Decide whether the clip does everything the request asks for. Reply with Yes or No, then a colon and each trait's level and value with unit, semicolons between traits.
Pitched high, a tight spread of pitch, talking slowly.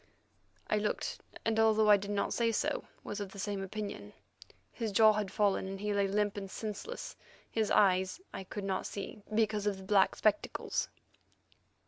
No: high, 205 Hz; narrow, 1.6 semitones; average, 175 wpm